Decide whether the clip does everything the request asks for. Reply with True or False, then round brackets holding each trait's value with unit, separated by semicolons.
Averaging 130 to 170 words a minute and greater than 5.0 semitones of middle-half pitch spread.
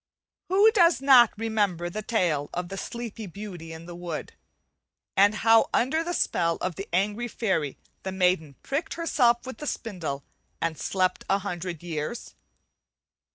True (155 wpm; 5.4 semitones)